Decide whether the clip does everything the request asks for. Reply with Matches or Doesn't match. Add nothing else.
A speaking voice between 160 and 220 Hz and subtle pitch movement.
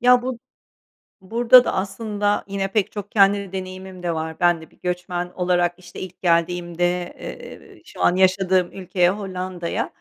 Matches